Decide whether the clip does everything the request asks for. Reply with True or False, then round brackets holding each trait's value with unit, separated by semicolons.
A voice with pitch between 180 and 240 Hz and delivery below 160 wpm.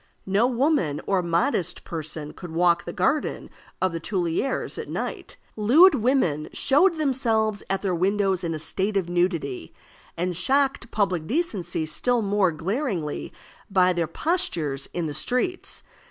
True (190 Hz; 145 wpm)